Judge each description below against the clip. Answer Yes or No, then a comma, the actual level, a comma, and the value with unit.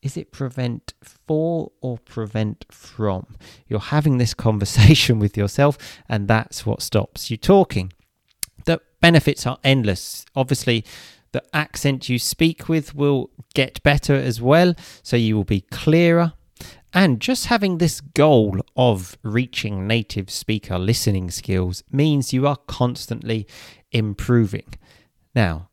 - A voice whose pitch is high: No, low, 125 Hz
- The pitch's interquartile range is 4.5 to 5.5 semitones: Yes, average, 5.0 semitones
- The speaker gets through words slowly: Yes, slow, 130 wpm